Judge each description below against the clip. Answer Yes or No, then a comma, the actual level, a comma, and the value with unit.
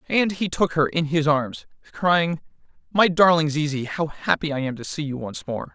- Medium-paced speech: No, fast, 210 wpm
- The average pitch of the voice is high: No, medium, 155 Hz